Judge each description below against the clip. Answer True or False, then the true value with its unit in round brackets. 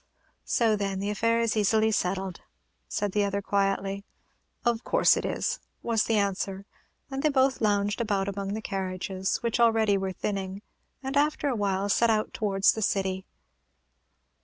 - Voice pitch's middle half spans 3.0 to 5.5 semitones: False (2.6 semitones)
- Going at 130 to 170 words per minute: True (160 wpm)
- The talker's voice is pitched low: False (205 Hz)